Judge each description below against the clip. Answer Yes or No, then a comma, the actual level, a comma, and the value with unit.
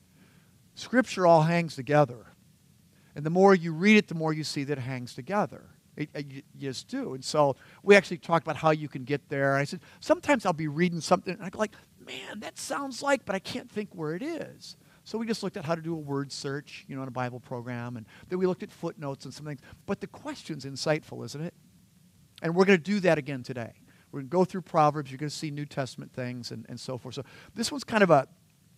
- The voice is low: No, medium, 155 Hz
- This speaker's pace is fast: Yes, fast, 250 wpm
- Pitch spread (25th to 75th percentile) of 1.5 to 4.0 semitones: No, average, 5.1 semitones